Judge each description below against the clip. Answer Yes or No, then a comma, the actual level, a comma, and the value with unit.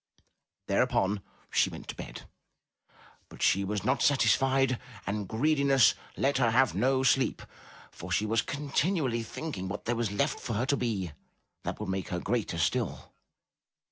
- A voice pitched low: Yes, low, 120 Hz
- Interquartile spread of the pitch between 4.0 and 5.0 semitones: Yes, average, 4.7 semitones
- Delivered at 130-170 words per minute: Yes, average, 160 wpm